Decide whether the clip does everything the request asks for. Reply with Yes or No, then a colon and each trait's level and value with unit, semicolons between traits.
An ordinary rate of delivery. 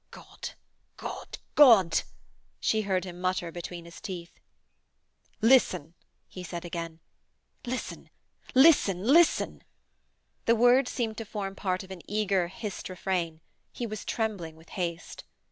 No: slow, 130 wpm